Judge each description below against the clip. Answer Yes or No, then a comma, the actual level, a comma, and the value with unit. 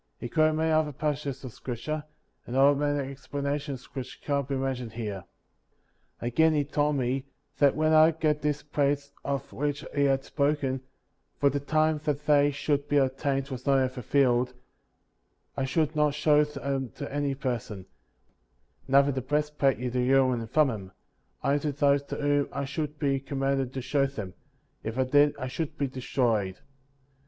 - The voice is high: No, medium, 140 Hz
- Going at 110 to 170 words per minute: No, average, 180 wpm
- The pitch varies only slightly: Yes, narrow, 2.1 semitones